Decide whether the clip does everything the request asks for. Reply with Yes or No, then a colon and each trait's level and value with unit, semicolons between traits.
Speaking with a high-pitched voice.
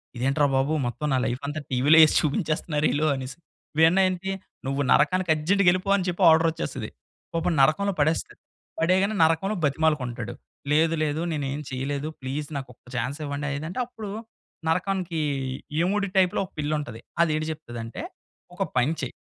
No: medium, 155 Hz